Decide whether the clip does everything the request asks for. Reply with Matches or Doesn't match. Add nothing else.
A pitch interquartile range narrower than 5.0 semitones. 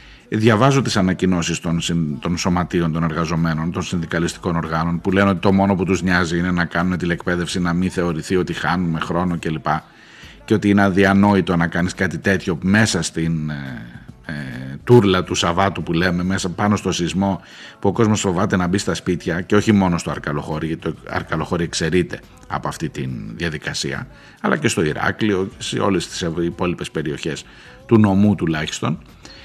Matches